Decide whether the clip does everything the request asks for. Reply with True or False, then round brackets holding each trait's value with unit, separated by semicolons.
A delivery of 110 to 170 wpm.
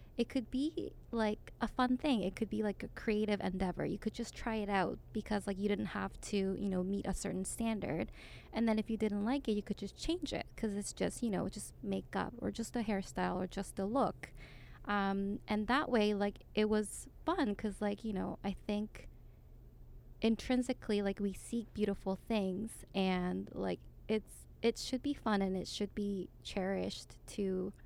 False (200 wpm)